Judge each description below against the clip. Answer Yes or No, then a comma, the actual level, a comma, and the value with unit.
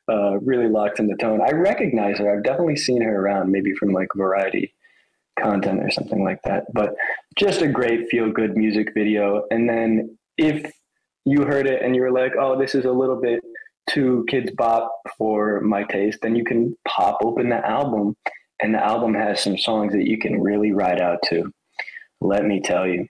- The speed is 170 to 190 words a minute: No, average, 200 wpm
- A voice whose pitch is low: Yes, low, 110 Hz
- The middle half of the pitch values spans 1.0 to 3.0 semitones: No, average, 3.8 semitones